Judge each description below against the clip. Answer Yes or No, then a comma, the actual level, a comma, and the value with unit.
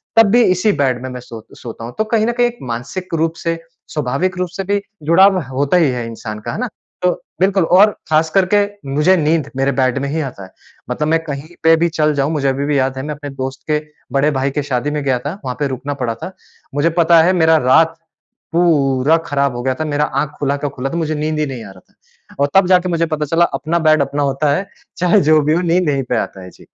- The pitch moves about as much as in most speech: Yes, average, 4.0 semitones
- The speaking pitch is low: No, medium, 150 Hz